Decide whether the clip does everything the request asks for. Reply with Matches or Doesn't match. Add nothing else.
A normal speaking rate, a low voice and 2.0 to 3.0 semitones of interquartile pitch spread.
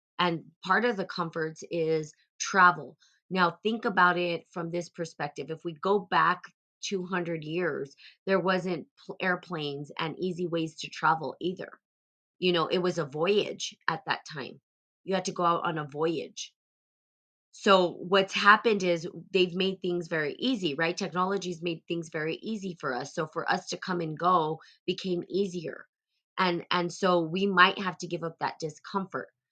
Doesn't match